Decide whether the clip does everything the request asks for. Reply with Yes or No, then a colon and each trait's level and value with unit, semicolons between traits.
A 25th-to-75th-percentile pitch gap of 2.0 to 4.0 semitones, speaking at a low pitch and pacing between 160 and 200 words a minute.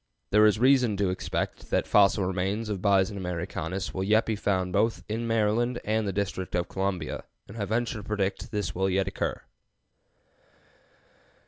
Yes: narrow, 2.5 semitones; low, 100 Hz; average, 175 wpm